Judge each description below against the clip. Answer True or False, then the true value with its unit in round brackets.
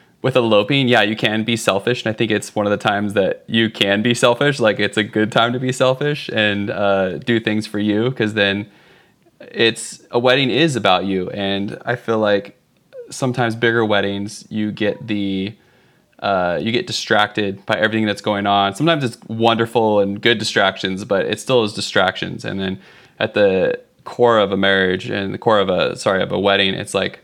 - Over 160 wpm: True (200 wpm)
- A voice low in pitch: True (110 Hz)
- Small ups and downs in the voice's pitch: False (3.1 semitones)